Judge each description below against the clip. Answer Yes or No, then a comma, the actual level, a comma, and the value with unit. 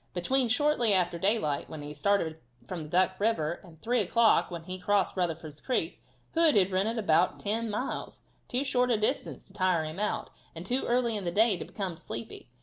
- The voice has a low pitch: No, high, 195 Hz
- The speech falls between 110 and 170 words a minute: No, average, 200 wpm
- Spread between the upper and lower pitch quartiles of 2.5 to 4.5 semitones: No, average, 5.3 semitones